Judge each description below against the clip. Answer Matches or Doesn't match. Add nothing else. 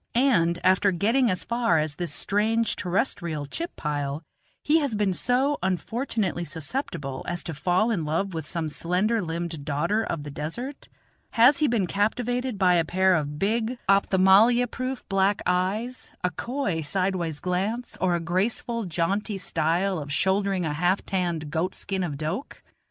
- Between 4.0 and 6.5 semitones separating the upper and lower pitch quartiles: Matches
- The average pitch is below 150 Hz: Doesn't match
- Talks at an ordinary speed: Matches